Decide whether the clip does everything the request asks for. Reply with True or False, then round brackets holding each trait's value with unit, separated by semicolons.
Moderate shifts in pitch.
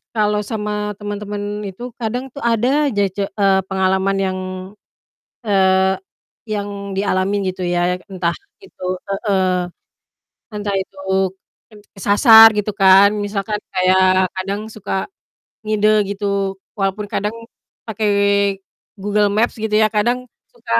False (1.9 semitones)